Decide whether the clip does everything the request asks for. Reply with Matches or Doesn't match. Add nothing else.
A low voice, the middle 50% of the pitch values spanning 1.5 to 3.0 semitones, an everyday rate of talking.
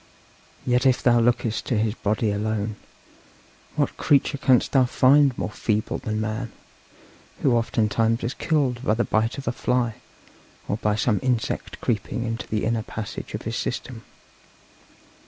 Matches